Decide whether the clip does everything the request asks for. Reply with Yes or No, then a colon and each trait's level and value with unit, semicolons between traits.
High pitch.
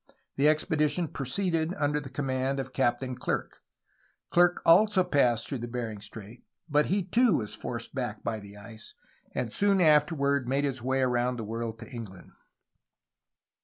No: low, 135 Hz